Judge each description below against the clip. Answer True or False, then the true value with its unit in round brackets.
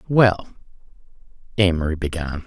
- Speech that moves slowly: True (75 wpm)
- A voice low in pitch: True (90 Hz)